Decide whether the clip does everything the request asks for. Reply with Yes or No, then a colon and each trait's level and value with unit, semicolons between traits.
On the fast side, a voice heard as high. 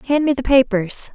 Yes: fast, 210 wpm; very high, 255 Hz